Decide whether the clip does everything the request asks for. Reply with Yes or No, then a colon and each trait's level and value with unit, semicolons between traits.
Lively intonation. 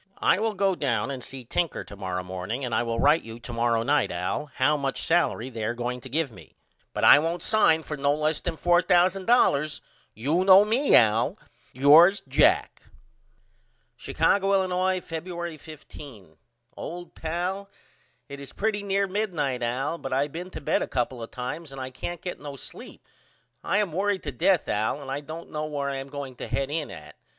Yes: wide, 5.7 semitones